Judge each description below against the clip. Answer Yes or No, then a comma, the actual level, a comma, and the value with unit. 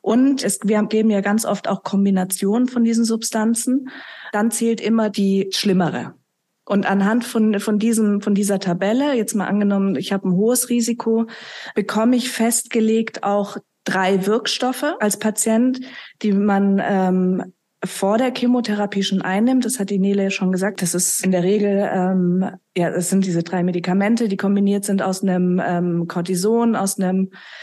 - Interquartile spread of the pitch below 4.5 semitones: Yes, average, 2.8 semitones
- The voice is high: Yes, high, 205 Hz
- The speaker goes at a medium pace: Yes, average, 165 wpm